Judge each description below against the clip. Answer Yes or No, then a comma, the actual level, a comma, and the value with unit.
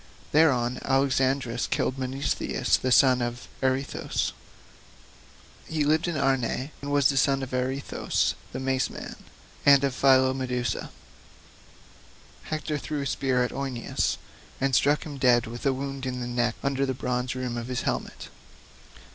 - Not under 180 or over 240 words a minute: No, average, 145 wpm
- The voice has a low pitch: Yes, low, 130 Hz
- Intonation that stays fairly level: Yes, narrow, 1.7 semitones